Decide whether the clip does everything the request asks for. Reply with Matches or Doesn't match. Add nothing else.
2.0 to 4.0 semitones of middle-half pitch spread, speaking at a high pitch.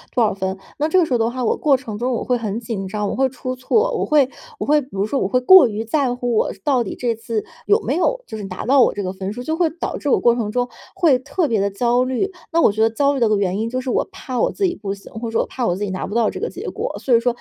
Doesn't match